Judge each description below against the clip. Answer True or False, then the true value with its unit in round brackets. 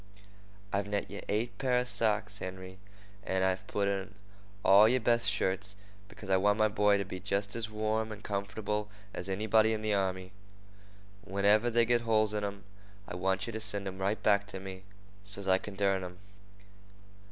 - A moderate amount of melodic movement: False (2.0 semitones)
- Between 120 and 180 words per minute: False (190 wpm)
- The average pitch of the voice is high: False (100 Hz)